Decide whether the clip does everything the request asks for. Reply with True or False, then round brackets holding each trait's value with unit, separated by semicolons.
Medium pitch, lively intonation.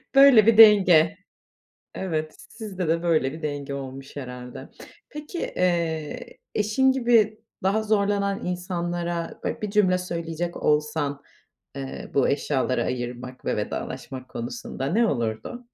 True (170 Hz; 6.6 semitones)